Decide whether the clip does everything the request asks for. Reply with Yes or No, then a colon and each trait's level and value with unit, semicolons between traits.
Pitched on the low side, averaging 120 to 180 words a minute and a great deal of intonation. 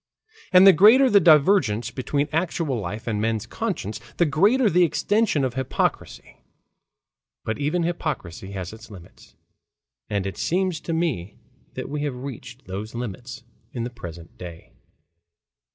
Yes: low, 130 Hz; average, 145 wpm; wide, 7.8 semitones